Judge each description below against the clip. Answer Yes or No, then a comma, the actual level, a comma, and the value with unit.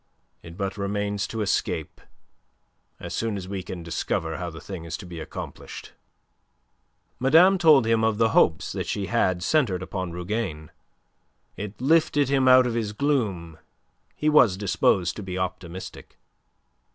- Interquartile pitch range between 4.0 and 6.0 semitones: Yes, average, 4.8 semitones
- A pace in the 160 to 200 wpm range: No, average, 150 wpm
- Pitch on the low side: Yes, low, 100 Hz